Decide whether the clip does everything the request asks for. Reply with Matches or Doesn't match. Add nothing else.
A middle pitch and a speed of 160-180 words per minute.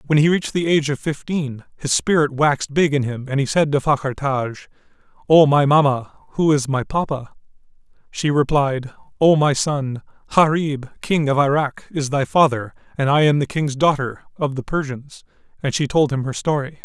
Doesn't match